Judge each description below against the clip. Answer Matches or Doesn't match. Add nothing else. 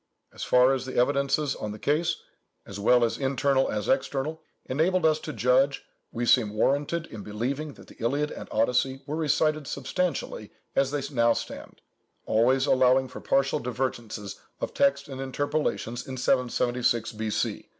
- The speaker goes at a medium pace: Matches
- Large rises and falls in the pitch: Doesn't match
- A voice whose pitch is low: Matches